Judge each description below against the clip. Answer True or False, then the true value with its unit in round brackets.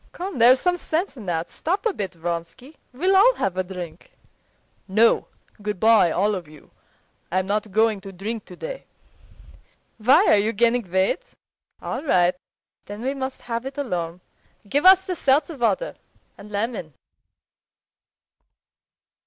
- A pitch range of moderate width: False (6.8 semitones)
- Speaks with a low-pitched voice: False (220 Hz)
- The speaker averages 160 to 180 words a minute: False (145 wpm)